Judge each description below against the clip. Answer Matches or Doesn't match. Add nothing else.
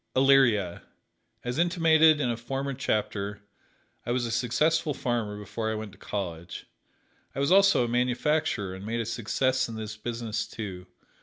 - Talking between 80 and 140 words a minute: Doesn't match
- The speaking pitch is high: Doesn't match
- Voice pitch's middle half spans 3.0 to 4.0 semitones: Doesn't match